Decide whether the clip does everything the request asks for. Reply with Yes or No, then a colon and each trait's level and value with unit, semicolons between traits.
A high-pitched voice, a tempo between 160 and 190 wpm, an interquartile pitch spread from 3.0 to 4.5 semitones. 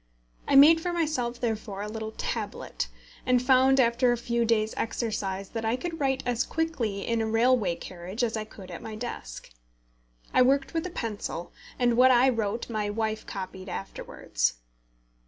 Yes: high, 230 Hz; average, 175 wpm; average, 3.4 semitones